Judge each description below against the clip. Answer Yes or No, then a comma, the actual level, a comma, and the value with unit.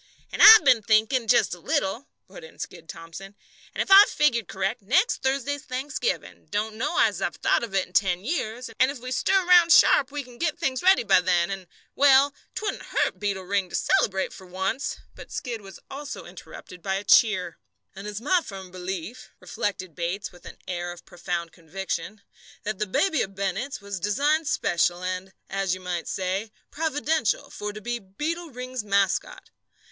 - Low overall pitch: No, high, 210 Hz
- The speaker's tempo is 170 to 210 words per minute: Yes, average, 190 wpm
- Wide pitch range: Yes, wide, 6.6 semitones